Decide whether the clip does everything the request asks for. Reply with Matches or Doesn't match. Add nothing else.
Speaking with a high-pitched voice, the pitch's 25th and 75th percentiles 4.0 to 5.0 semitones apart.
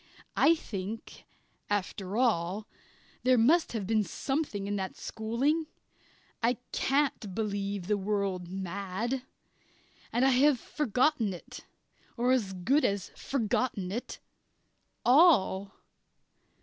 Matches